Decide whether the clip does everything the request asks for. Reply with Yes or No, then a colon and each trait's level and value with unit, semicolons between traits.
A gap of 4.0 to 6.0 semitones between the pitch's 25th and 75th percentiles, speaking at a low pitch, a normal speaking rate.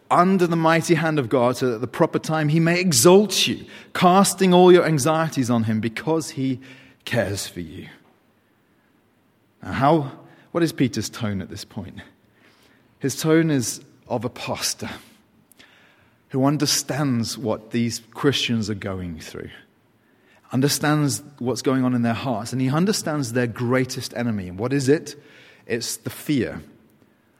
Yes: average, 5.2 semitones; low, 130 Hz; average, 155 wpm